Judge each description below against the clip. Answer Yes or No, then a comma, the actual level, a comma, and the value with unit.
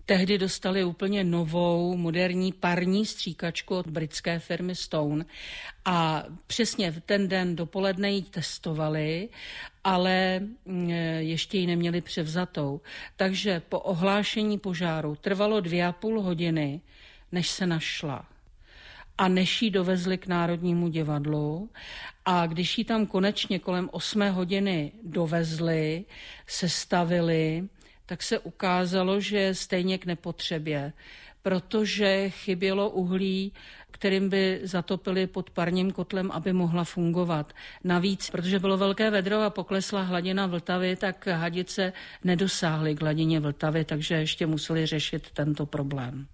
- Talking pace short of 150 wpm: Yes, average, 120 wpm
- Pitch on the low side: No, medium, 180 Hz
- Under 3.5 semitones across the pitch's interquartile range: Yes, narrow, 2.5 semitones